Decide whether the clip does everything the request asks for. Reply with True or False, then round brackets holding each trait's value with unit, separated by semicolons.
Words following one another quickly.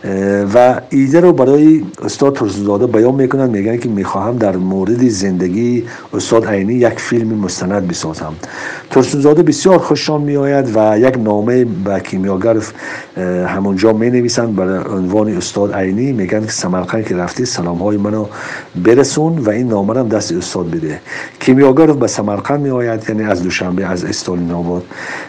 False (145 wpm)